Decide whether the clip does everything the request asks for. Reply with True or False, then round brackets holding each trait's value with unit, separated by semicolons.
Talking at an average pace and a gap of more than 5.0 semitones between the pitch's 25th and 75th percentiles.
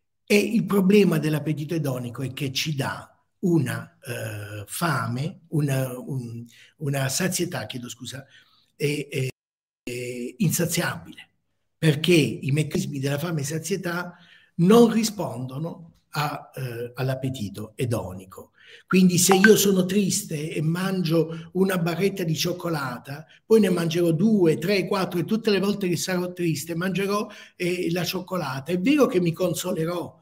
True (135 wpm; 5.4 semitones)